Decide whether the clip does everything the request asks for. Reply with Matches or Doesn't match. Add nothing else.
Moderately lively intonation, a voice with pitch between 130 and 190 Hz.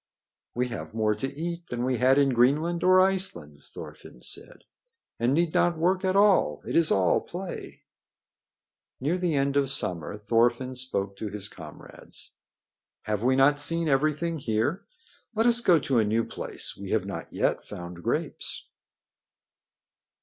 Doesn't match